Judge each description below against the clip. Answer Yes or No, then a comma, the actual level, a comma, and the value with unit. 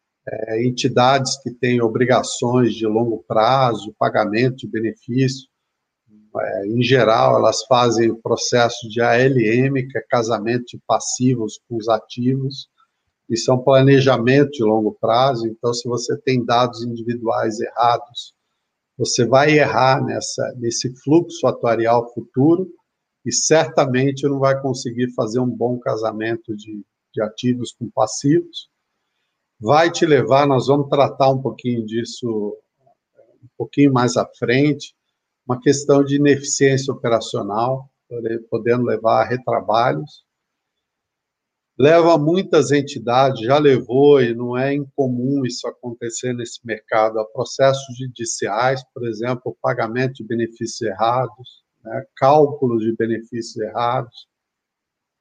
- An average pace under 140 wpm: Yes, average, 125 wpm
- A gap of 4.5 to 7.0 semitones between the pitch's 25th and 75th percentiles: No, average, 2.7 semitones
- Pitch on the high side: No, low, 125 Hz